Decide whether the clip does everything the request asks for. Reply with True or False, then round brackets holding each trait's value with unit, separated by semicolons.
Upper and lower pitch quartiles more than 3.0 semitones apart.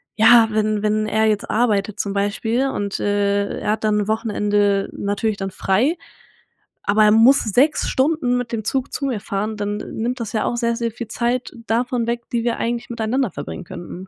False (2.6 semitones)